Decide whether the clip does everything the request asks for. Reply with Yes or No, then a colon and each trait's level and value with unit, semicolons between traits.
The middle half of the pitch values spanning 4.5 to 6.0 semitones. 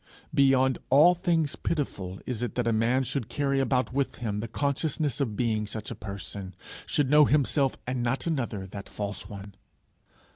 Yes: average, 4.8 semitones